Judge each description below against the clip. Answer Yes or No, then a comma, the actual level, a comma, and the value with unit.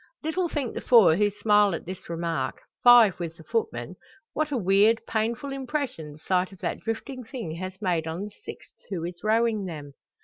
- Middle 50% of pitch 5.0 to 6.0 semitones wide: Yes, wide, 5.5 semitones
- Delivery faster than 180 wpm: Yes, average, 195 wpm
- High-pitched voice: Yes, high, 205 Hz